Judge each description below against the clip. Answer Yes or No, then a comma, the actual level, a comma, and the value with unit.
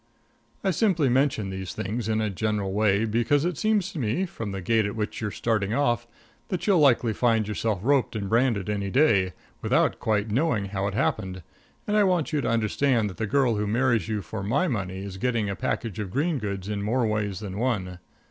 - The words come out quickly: Yes, fast, 215 wpm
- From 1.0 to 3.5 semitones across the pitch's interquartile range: No, average, 4.5 semitones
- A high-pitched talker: No, low, 110 Hz